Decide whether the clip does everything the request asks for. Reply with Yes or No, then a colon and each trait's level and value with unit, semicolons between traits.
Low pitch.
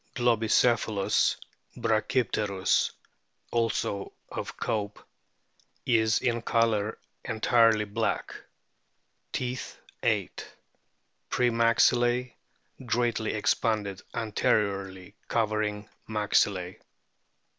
Yes: low, 110 Hz